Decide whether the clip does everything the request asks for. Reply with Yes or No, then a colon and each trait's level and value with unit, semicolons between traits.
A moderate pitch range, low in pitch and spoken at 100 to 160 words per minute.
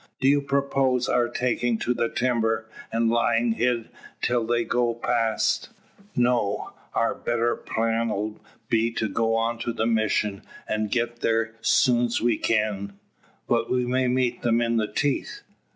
No: narrow, 1.4 semitones; low, 115 Hz; average, 155 wpm